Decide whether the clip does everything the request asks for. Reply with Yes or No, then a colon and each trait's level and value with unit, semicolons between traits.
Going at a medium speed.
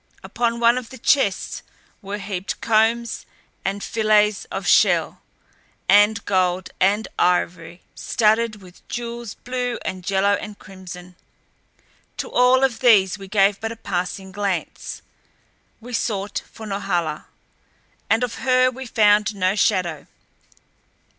No: slow, 125 wpm